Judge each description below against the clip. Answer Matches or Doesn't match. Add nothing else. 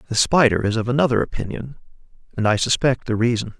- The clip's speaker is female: Doesn't match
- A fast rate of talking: Doesn't match